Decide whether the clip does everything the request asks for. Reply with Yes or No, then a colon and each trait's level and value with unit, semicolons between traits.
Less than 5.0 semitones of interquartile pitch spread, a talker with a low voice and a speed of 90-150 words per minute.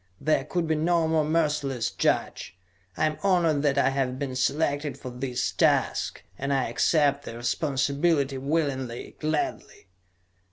No: average, 2.9 semitones; medium, 145 Hz; average, 145 wpm